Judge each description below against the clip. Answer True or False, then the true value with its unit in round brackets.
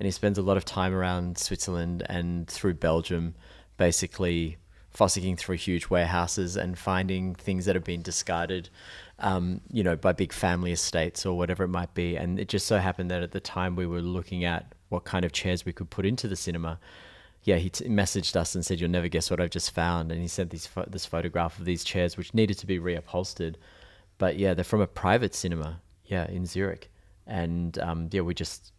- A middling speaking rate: False (215 wpm)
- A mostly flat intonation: True (1.6 semitones)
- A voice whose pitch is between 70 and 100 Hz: True (90 Hz)